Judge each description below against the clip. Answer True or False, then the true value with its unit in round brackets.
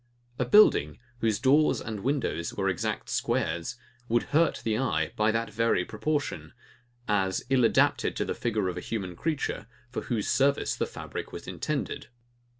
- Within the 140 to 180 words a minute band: True (160 wpm)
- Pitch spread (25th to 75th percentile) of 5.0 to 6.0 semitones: True (5.5 semitones)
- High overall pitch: False (110 Hz)